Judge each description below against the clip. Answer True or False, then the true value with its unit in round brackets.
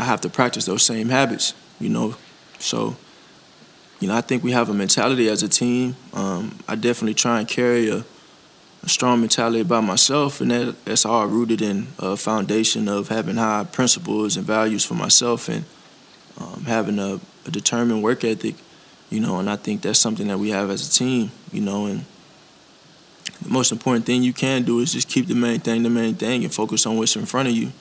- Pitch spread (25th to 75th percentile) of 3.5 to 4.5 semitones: False (2.4 semitones)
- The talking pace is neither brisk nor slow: False (210 wpm)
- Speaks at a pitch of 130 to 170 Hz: False (115 Hz)